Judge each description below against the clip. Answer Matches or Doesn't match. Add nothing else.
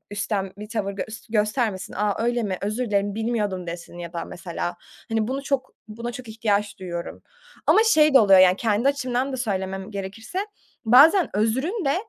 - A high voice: Matches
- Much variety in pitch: Doesn't match